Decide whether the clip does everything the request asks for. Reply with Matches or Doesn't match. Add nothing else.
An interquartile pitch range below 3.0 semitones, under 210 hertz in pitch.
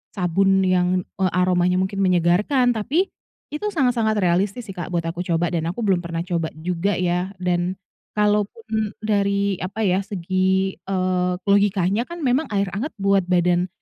Matches